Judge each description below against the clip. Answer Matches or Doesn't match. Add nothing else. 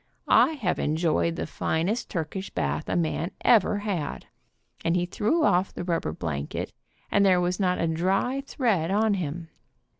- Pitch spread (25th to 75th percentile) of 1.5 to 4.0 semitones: Matches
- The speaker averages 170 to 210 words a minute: Doesn't match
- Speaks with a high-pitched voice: Doesn't match